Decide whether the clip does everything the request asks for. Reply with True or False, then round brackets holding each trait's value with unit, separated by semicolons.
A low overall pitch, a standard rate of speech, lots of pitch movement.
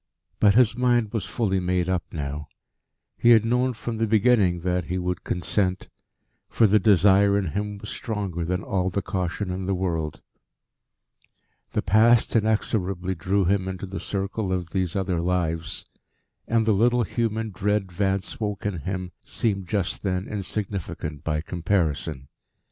False (95 Hz; 155 wpm; 2.9 semitones)